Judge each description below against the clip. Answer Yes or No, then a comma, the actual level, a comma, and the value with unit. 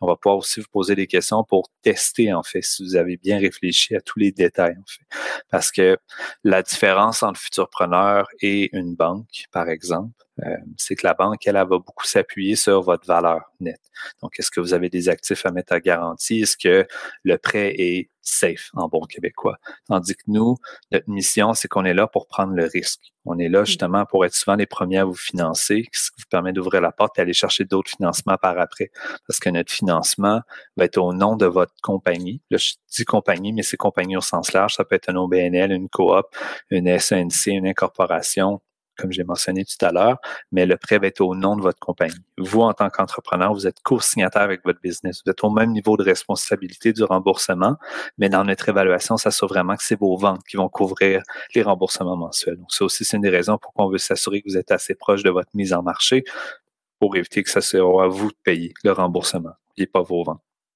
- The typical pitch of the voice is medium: No, very low, 95 Hz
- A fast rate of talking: Yes, fast, 225 wpm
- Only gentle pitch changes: Yes, narrow, 1.9 semitones